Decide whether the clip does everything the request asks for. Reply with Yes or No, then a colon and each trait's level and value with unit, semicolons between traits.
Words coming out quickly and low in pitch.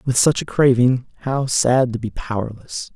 No: average, 185 wpm; low, 125 Hz